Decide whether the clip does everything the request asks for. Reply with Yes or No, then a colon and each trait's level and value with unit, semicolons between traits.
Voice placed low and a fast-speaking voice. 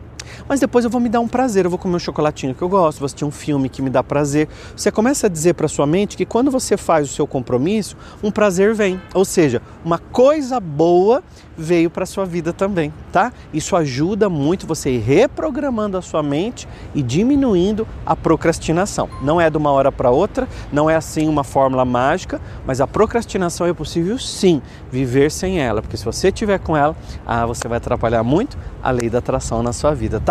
No: medium, 160 Hz; fast, 210 wpm